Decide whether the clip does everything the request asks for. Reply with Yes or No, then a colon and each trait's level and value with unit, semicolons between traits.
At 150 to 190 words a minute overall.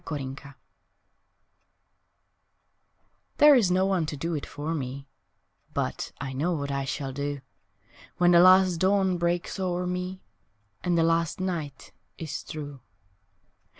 No: slow, 135 wpm